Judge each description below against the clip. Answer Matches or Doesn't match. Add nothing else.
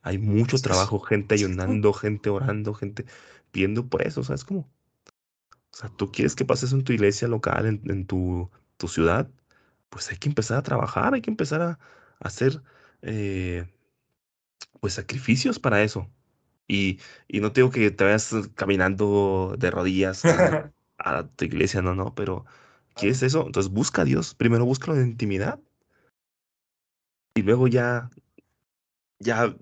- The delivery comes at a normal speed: Matches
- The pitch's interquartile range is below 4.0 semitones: Doesn't match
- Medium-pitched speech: Doesn't match